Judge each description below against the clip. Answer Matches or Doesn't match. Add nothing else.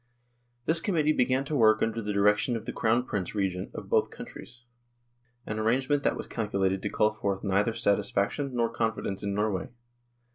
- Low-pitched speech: Matches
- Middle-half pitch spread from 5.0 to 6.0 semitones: Doesn't match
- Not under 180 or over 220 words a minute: Matches